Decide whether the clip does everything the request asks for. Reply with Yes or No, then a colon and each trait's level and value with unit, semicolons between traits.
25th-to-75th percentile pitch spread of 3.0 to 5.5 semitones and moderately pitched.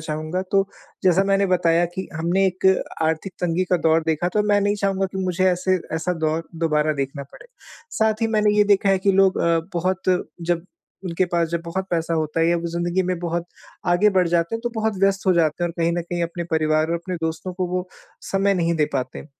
No: narrow, 2.5 semitones; medium, 175 Hz